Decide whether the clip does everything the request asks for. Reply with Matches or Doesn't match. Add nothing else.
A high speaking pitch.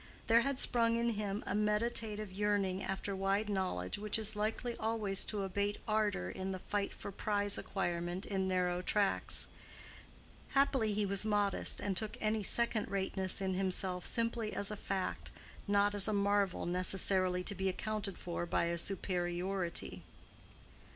Matches